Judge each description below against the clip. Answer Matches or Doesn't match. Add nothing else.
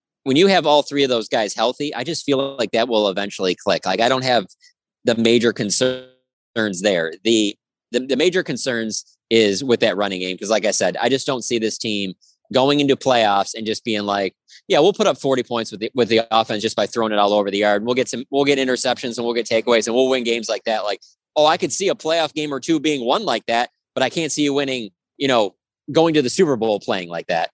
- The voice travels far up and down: Doesn't match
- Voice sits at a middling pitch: Doesn't match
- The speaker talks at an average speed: Doesn't match